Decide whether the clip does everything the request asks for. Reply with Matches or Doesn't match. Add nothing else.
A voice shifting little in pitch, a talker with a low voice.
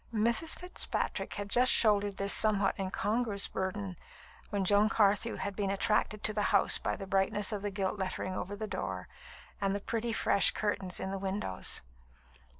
Doesn't match